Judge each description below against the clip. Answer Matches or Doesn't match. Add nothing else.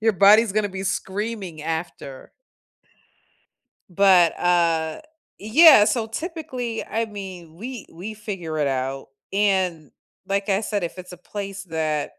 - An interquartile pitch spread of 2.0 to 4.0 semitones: Doesn't match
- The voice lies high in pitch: Matches